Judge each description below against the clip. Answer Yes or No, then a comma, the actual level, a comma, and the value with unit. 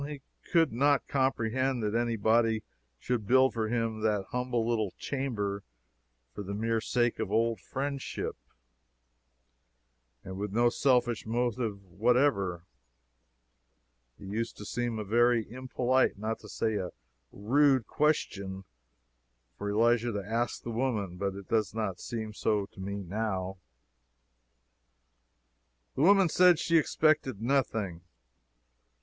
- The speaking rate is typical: No, slow, 130 wpm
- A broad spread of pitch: No, average, 3.8 semitones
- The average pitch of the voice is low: Yes, low, 115 Hz